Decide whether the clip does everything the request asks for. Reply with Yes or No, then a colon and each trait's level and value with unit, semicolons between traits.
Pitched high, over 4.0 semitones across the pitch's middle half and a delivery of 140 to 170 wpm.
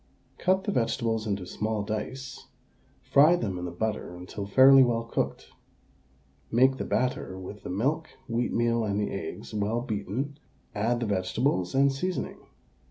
No: low, 115 Hz; average, 4.5 semitones; average, 150 wpm